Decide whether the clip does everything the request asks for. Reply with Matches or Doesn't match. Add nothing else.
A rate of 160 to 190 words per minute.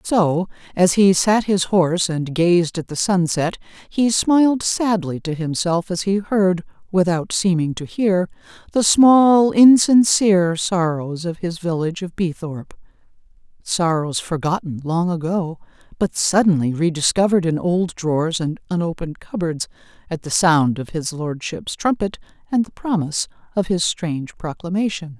Doesn't match